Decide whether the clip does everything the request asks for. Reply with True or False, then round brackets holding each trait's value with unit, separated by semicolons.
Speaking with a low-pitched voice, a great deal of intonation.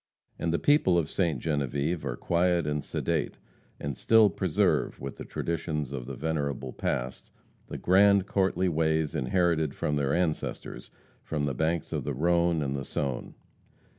False (80 Hz; 3.5 semitones)